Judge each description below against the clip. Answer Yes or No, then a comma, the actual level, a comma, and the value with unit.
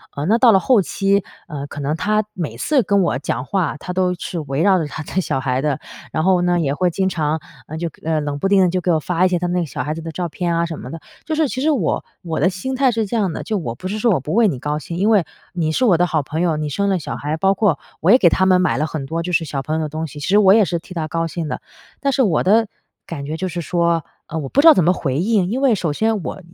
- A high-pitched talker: No, medium, 175 Hz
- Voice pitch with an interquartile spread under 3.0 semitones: No, average, 3.9 semitones